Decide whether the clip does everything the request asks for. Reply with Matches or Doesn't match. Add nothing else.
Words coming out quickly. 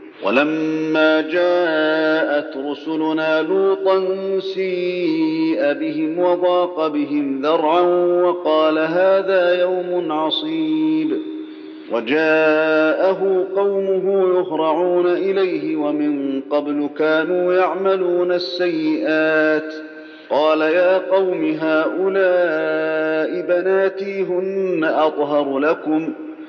Doesn't match